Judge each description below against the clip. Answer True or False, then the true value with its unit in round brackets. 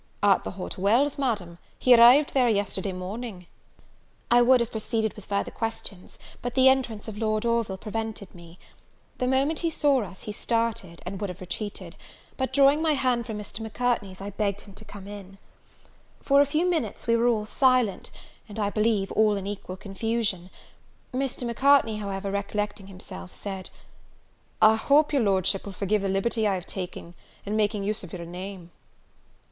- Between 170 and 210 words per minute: True (175 wpm)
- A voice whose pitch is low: False (215 Hz)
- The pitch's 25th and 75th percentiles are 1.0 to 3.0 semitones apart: False (3.6 semitones)